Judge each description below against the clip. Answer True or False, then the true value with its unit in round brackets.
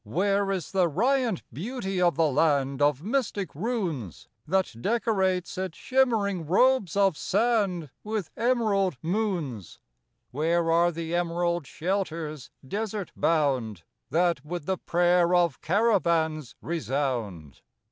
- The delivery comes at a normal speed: False (115 wpm)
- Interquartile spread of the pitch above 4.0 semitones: True (4.5 semitones)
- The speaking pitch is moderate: True (175 Hz)